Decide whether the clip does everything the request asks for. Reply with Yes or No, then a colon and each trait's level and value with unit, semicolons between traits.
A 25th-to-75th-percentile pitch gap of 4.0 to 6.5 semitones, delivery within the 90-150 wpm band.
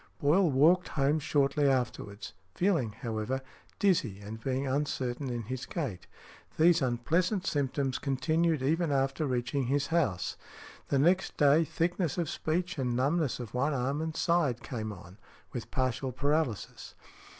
Yes: average, 4.4 semitones; average, 140 wpm